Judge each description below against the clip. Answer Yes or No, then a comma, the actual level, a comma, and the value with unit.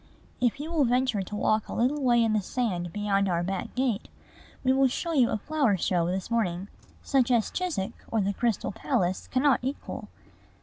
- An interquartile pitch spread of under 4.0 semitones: No, average, 5.0 semitones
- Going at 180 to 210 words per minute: Yes, average, 190 wpm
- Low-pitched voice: No, high, 235 Hz